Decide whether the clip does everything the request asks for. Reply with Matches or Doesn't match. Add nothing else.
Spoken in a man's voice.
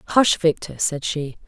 Doesn't match